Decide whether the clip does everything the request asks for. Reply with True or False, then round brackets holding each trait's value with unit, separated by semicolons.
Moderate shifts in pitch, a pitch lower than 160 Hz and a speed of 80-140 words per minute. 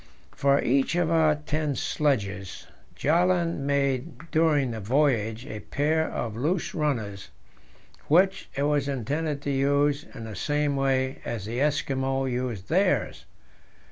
True (3.4 semitones; 140 Hz; 135 wpm)